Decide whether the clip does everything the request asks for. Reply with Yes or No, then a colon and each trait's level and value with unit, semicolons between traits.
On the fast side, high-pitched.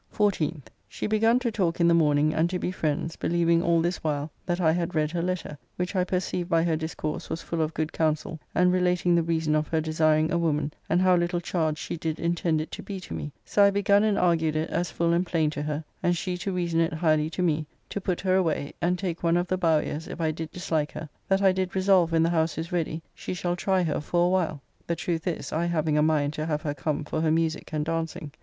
No: fast, 255 wpm; medium, 165 Hz